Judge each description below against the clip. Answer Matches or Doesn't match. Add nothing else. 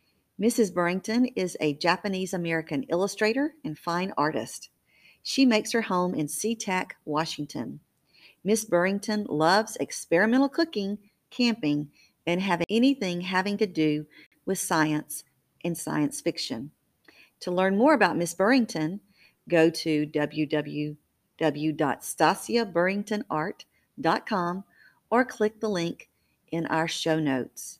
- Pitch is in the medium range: Matches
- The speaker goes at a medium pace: Doesn't match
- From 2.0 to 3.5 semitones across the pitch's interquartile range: Doesn't match